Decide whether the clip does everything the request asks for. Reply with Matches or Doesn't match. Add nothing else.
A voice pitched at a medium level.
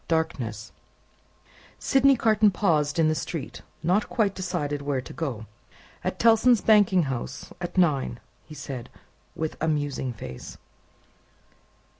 Matches